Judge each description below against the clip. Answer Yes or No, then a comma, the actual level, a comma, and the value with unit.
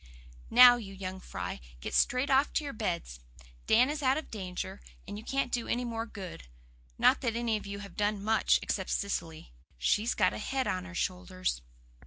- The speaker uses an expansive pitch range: No, average, 4.7 semitones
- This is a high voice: Yes, high, 210 Hz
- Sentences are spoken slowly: No, average, 195 wpm